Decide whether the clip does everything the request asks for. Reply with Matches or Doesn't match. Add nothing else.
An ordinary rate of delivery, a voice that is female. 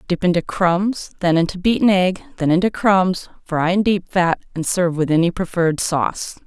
Matches